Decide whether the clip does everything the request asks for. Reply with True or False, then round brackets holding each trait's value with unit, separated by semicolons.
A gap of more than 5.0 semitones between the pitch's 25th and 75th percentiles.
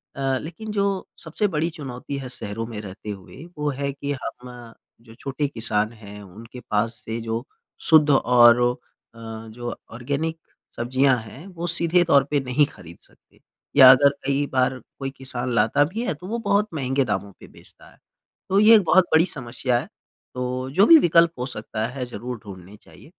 True (5.4 semitones)